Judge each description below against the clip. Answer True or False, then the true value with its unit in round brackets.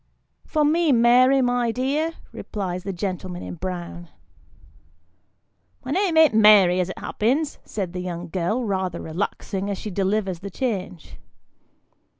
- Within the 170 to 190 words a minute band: False (150 wpm)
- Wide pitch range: True (5.7 semitones)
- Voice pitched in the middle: False (200 Hz)